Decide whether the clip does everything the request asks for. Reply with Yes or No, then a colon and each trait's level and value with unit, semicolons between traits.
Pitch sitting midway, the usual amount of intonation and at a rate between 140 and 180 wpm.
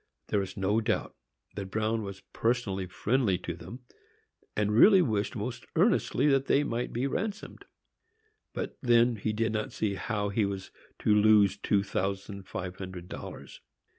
No: low, 105 Hz; average, 3.4 semitones; average, 160 wpm